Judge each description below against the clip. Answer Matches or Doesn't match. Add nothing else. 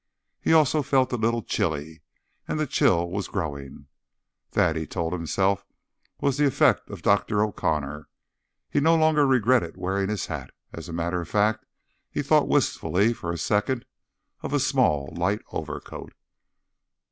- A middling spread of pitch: Doesn't match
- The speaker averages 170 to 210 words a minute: Doesn't match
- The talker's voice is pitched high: Doesn't match